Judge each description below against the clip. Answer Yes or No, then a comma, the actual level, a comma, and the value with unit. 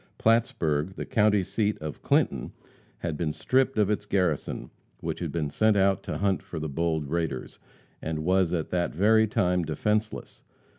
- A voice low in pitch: Yes, very low, 90 Hz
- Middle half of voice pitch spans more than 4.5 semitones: Yes, average, 4.9 semitones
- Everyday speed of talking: Yes, average, 165 wpm